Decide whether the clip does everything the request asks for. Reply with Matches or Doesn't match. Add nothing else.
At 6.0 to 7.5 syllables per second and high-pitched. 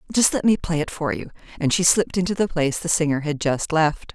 Doesn't match